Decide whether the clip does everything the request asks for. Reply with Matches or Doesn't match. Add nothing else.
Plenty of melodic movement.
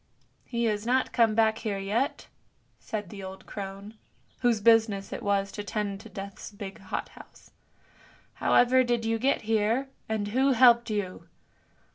Doesn't match